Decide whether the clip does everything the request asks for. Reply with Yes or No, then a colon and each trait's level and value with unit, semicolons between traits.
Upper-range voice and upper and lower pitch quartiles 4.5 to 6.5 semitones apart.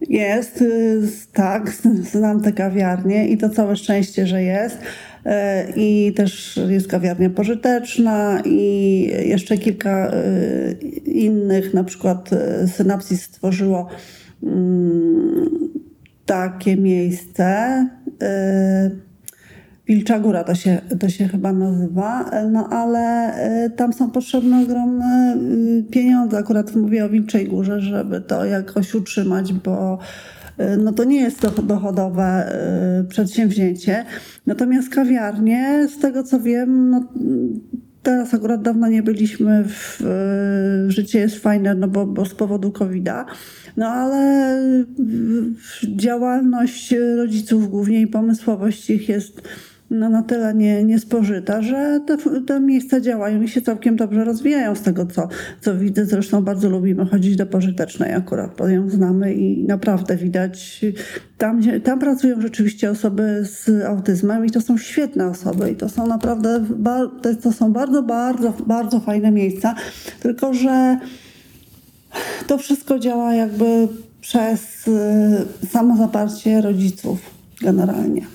No: high, 215 Hz; average, 3.4 semitones